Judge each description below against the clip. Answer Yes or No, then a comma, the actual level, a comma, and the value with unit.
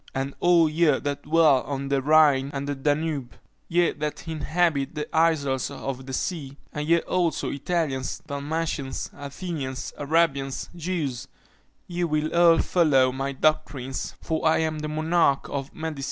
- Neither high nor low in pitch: Yes, medium, 150 Hz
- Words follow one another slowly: No, average, 150 wpm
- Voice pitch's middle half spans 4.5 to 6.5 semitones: No, average, 3.0 semitones